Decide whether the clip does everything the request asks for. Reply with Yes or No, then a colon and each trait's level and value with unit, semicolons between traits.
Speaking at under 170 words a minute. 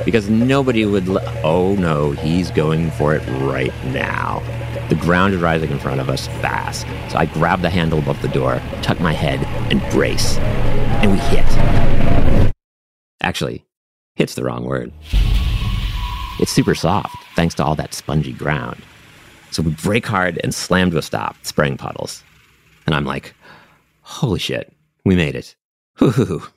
Yes: average, 160 wpm